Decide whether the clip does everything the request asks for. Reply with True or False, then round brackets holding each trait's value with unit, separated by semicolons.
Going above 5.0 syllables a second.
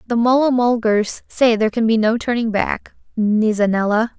False (4.9 syllables/s)